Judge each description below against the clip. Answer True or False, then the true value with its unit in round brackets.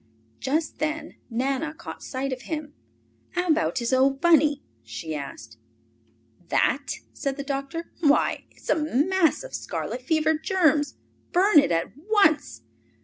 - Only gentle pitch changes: False (3.5 semitones)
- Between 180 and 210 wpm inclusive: False (140 wpm)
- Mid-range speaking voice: False (290 Hz)